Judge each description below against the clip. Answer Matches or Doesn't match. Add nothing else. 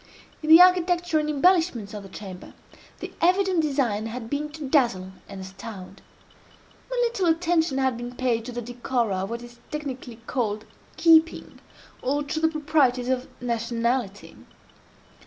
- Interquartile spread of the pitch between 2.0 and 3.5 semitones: Doesn't match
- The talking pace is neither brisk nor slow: Matches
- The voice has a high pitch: Matches